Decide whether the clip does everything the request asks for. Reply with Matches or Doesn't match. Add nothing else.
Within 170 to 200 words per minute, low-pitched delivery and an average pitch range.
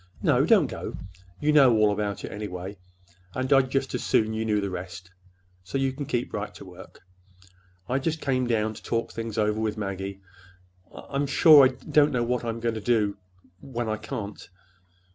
Matches